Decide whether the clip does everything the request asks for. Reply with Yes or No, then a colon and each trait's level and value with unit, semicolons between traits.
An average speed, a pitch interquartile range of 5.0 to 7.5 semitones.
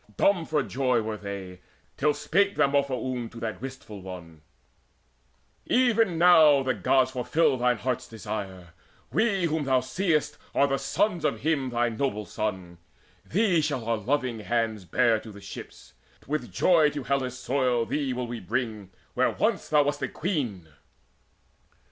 Yes: average, 155 wpm; average, 5.3 semitones